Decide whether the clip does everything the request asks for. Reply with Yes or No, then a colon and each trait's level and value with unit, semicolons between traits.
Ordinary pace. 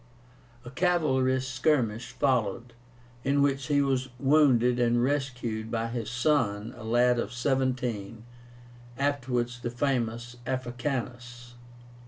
No: slow, 110 wpm